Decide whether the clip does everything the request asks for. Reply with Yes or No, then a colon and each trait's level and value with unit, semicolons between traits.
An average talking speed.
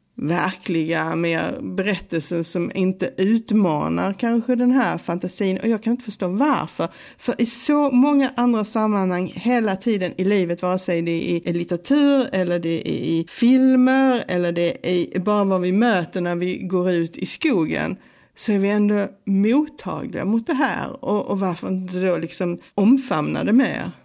Yes: average, 170 wpm